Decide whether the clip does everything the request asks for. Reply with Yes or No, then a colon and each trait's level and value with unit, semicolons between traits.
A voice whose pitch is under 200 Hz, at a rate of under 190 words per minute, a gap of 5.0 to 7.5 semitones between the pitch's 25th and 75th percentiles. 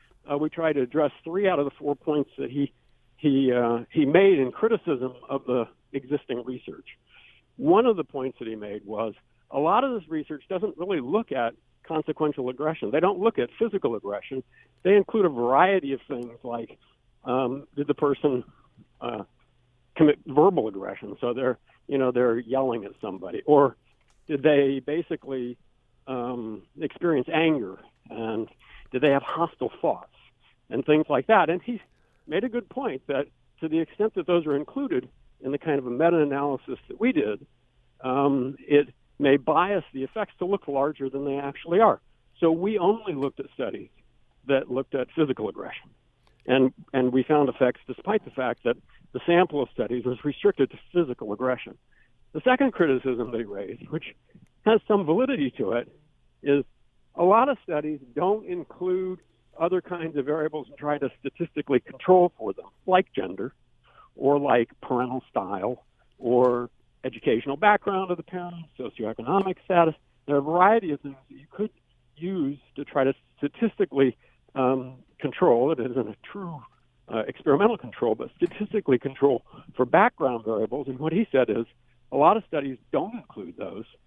Yes: medium, 140 Hz; average, 170 wpm; average, 5.3 semitones